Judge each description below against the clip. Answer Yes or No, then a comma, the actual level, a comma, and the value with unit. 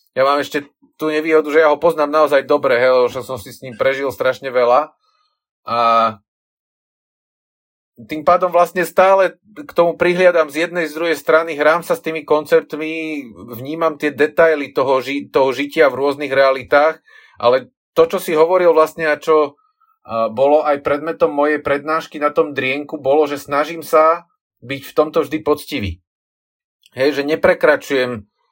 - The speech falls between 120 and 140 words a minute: No, average, 160 wpm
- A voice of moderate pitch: Yes, medium, 155 Hz